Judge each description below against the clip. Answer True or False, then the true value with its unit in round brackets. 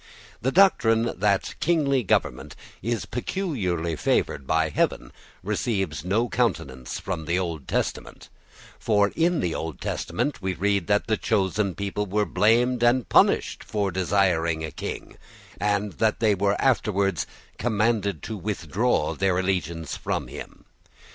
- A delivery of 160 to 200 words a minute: False (135 wpm)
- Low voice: True (100 Hz)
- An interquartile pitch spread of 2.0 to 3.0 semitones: False (4.5 semitones)